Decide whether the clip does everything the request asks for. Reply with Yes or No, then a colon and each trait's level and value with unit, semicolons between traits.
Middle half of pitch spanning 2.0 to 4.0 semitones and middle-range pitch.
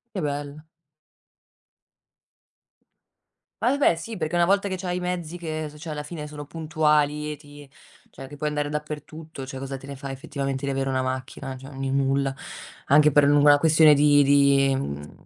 Yes: narrow, 2.3 semitones; medium, 145 Hz